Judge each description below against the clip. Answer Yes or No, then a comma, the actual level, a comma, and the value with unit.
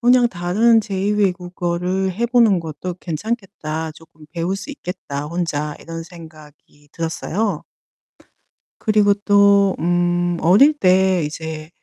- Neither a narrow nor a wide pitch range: Yes, average, 3.8 semitones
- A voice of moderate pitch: Yes, medium, 180 Hz